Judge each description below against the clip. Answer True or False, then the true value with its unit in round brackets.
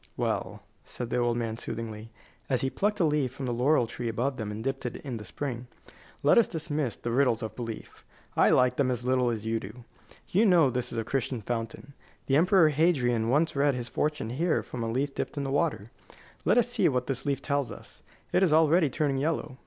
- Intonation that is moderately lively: True (3.8 semitones)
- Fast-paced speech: True (225 wpm)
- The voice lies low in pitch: True (130 Hz)